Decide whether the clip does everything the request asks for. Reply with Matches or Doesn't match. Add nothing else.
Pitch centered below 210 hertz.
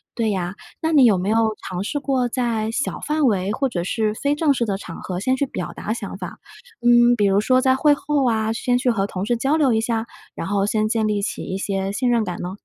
Doesn't match